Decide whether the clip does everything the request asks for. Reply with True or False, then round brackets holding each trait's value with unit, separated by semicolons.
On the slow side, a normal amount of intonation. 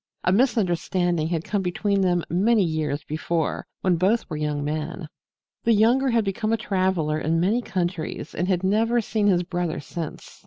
False (170 wpm; 4.3 semitones)